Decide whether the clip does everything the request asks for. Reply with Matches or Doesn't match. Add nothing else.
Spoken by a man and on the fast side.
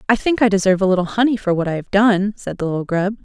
Doesn't match